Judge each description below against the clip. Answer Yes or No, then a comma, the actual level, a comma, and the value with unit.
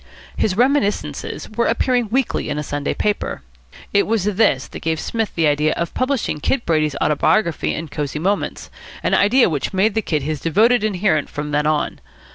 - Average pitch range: No, wide, 6.3 semitones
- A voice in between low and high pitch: Yes, medium, 180 Hz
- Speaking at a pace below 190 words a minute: Yes, average, 180 wpm